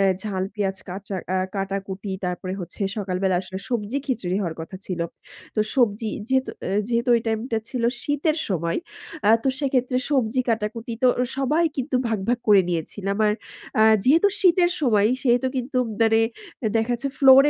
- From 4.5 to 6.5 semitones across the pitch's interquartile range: Yes, average, 4.9 semitones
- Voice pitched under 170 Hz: No, high, 225 Hz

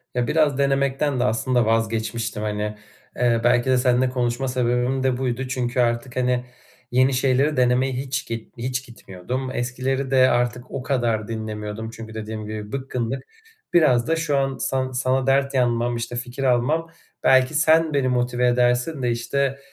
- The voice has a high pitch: No, low, 125 Hz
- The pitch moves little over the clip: Yes, narrow, 2.0 semitones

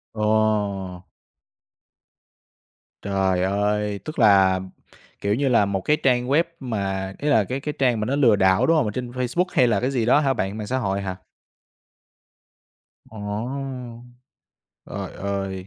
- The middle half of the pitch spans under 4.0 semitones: No, average, 4.4 semitones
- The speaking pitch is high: No, low, 105 Hz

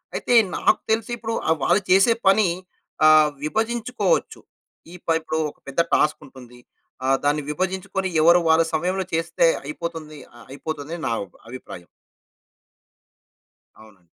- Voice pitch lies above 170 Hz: No, medium, 160 Hz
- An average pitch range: Yes, average, 4.3 semitones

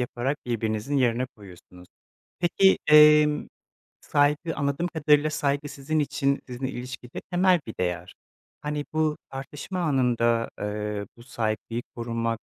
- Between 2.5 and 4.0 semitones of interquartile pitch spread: No, average, 4.5 semitones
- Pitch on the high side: No, low, 135 Hz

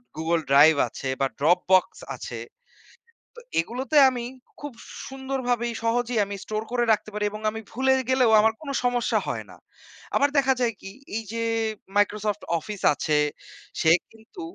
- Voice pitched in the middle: No, high, 225 Hz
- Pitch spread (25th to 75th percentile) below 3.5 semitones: No, average, 3.8 semitones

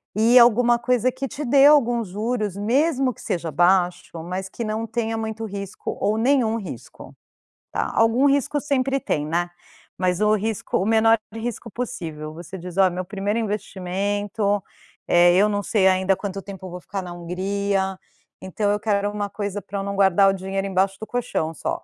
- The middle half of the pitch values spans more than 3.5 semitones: No, average, 3.2 semitones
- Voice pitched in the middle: No, high, 205 Hz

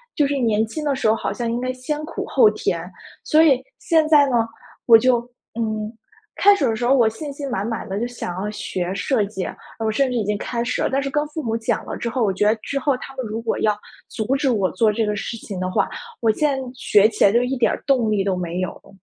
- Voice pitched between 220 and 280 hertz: Yes, high, 230 Hz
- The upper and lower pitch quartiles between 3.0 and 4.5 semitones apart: Yes, average, 4.2 semitones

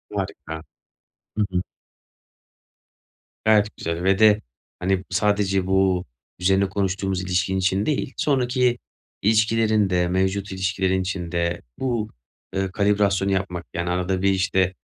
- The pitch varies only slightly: Yes, narrow, 2.1 semitones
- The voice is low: Yes, very low, 95 Hz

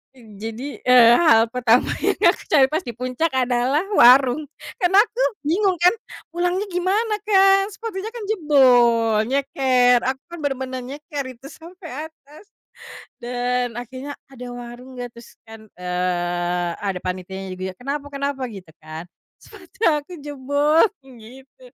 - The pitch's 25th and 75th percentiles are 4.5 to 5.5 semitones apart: Yes, average, 5.2 semitones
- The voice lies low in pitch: No, very high, 260 Hz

